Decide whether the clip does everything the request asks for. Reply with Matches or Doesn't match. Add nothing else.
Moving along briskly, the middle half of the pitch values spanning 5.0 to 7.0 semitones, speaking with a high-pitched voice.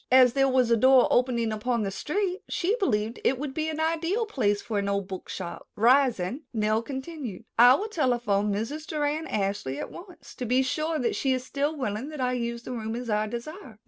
Matches